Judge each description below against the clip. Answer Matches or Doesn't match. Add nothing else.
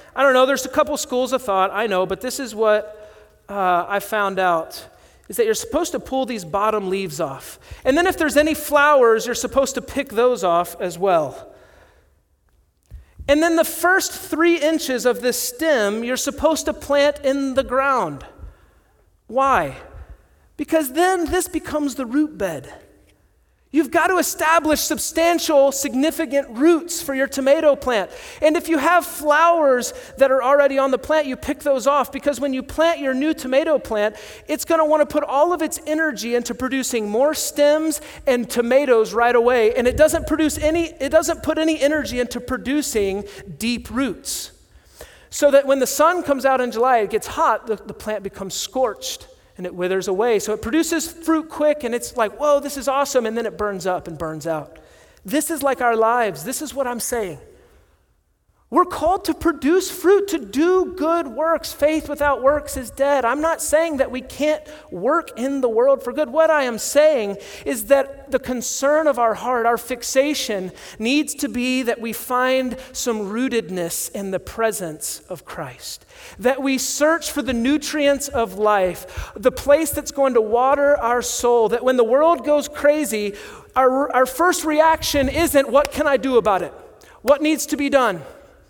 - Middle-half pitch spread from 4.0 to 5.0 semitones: Matches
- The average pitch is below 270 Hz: Doesn't match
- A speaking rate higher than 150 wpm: Matches